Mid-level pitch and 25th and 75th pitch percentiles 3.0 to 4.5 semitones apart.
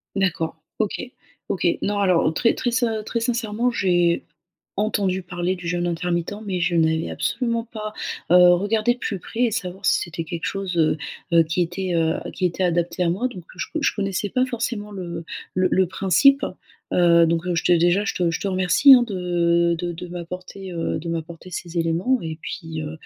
Yes: medium, 180 Hz; average, 3.3 semitones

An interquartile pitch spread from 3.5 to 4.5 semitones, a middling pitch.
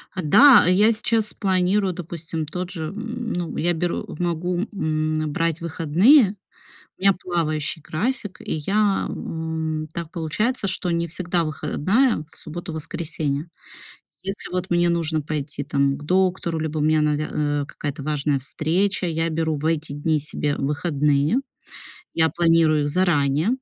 No: average, 3.1 semitones; medium, 165 Hz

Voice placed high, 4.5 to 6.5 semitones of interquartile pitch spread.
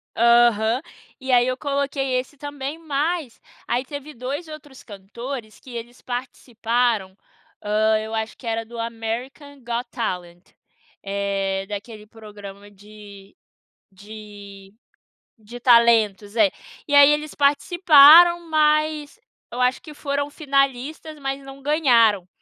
Yes: high, 245 Hz; average, 4.9 semitones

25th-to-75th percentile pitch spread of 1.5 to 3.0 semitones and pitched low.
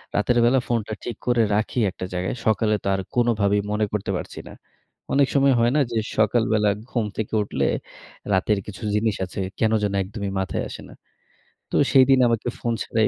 Yes: average, 2.7 semitones; low, 110 Hz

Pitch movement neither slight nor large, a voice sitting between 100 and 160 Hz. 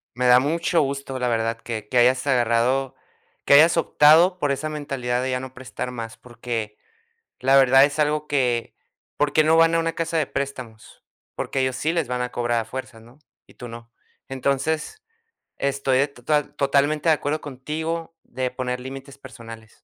Yes: average, 3.3 semitones; low, 135 Hz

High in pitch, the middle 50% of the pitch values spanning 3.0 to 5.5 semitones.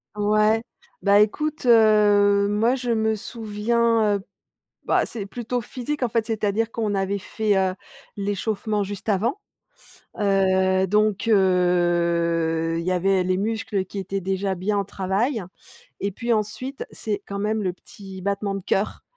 No: high, 205 Hz; narrow, 2.5 semitones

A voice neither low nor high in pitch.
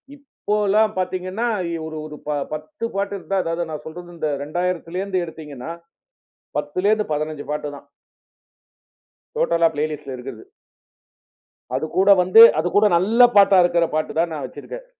Yes: medium, 170 Hz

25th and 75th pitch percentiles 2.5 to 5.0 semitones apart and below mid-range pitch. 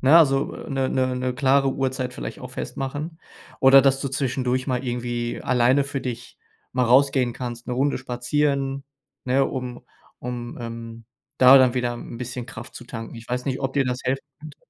No: narrow, 1.8 semitones; low, 130 Hz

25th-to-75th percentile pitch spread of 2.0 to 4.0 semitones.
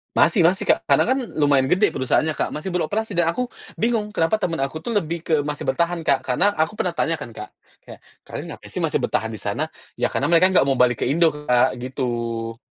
No: wide, 5.6 semitones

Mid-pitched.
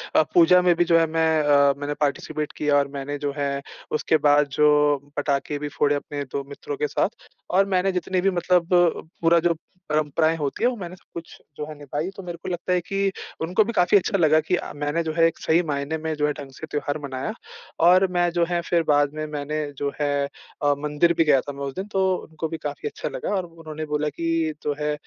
Yes: medium, 155 Hz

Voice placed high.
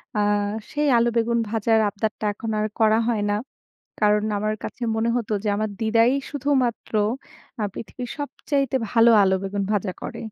Yes: high, 225 Hz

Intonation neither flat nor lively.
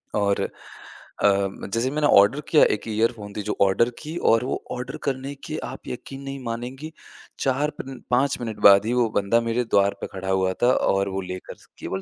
Yes: average, 4.9 semitones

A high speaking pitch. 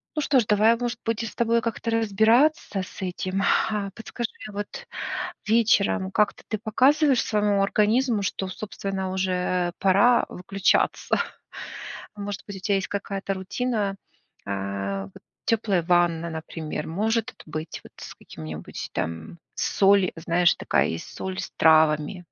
Yes: high, 195 Hz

